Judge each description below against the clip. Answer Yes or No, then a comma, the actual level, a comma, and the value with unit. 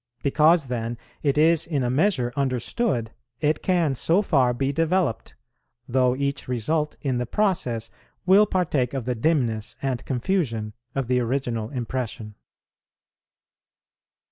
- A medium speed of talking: No, slow, 130 wpm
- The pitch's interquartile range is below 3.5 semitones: No, average, 4.7 semitones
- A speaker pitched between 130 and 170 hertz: Yes, low, 135 Hz